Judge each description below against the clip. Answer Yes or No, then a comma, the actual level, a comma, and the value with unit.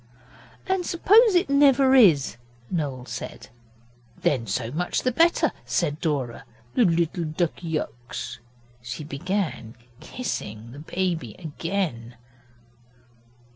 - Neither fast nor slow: No, slow, 100 wpm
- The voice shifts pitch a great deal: Yes, wide, 8.7 semitones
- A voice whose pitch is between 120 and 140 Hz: No, medium, 160 Hz